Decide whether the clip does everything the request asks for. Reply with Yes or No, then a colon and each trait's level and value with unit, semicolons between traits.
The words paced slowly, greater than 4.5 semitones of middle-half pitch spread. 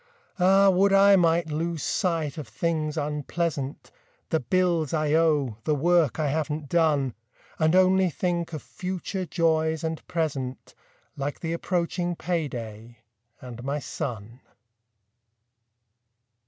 No: slow, 120 wpm; average, 3.3 semitones